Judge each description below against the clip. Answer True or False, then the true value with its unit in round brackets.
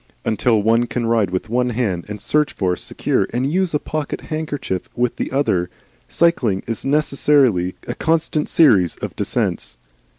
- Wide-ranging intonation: True (6.6 semitones)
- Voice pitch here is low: True (120 Hz)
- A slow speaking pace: False (160 wpm)